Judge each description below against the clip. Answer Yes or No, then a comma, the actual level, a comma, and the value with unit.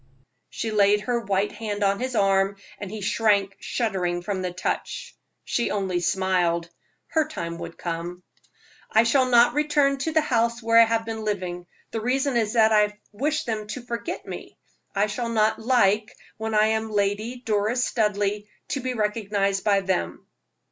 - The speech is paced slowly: No, average, 170 wpm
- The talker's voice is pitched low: No, high, 215 Hz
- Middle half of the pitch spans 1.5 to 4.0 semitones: Yes, average, 3.0 semitones